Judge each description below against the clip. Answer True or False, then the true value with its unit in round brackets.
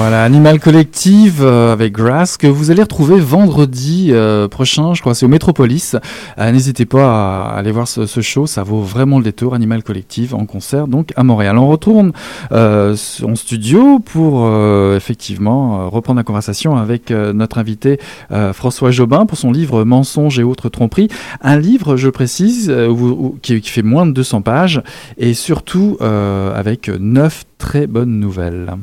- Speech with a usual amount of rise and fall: True (4.9 semitones)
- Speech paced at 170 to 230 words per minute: True (180 wpm)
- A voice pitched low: True (125 Hz)